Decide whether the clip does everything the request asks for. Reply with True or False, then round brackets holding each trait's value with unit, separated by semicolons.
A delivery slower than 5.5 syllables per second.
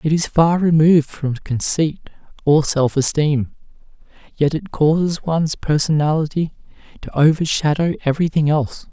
True (5.0 syllables/s)